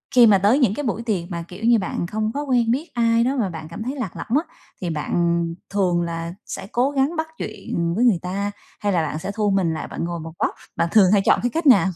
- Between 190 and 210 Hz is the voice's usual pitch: Yes, high, 205 Hz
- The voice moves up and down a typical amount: No, wide, 5.7 semitones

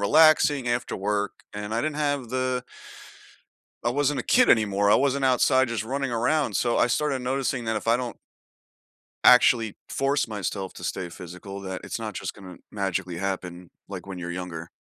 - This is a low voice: Yes, low, 115 Hz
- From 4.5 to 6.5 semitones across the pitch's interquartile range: Yes, average, 5.2 semitones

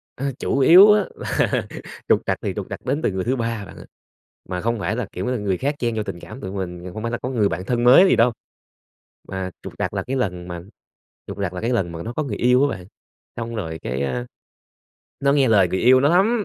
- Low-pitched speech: Yes, low, 115 Hz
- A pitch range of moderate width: No, wide, 5.8 semitones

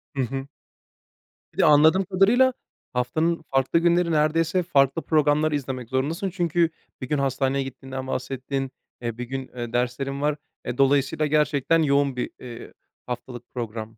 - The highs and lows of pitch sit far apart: No, average, 3.6 semitones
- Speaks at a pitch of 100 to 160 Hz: Yes, medium, 140 Hz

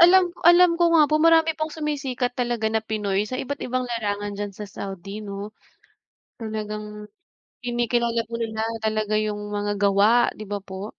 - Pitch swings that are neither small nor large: Yes, average, 3.2 semitones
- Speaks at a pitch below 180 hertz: No, high, 220 Hz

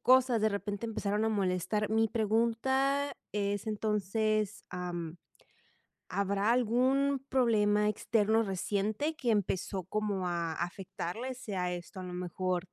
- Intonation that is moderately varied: Yes, average, 3.3 semitones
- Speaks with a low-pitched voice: No, high, 210 Hz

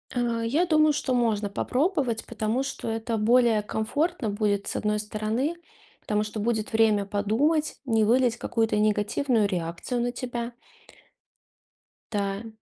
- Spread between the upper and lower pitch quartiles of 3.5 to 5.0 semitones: No, average, 2.9 semitones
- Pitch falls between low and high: No, high, 225 Hz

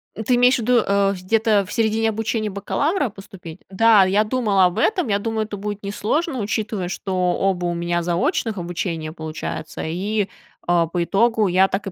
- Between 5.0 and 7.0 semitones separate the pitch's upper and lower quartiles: No, average, 3.7 semitones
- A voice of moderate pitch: No, high, 200 Hz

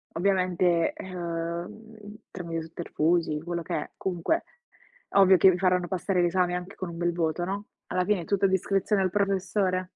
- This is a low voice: No, medium, 180 Hz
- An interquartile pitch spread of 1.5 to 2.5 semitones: Yes, narrow, 2.1 semitones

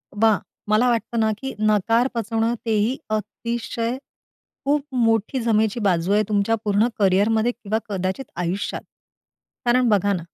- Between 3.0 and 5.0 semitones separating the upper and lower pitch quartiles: No, narrow, 2.4 semitones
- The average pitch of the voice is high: Yes, high, 220 Hz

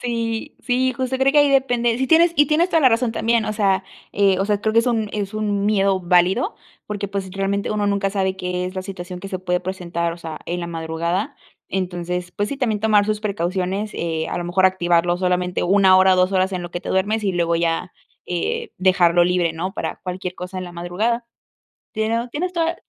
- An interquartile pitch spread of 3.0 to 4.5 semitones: Yes, average, 3.6 semitones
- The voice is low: No, high, 195 Hz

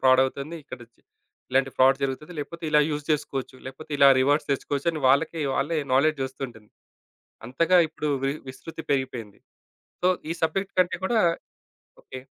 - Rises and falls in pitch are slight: No, average, 3.2 semitones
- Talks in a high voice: No, medium, 140 Hz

